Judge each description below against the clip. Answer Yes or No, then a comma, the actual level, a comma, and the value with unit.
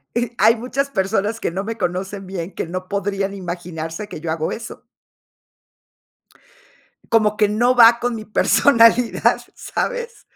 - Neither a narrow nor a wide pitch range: Yes, average, 3.9 semitones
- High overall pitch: Yes, high, 210 Hz